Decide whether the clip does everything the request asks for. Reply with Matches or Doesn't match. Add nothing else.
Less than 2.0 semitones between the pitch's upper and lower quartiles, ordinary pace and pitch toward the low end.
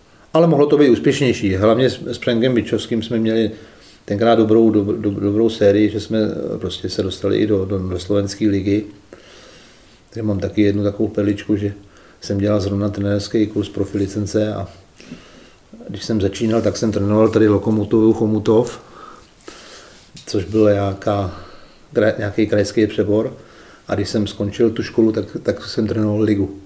Matches